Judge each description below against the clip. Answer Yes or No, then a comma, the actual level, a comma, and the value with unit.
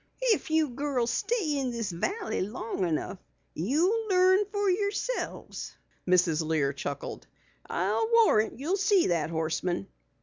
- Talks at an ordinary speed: No, slow, 130 wpm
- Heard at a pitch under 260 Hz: No, very high, 275 Hz